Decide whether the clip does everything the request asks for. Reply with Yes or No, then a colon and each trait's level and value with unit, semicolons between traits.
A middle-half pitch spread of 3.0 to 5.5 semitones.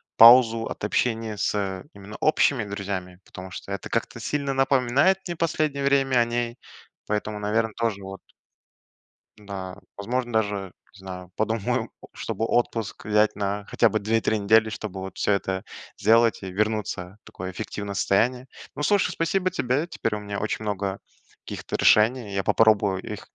Yes: average, 3.3 semitones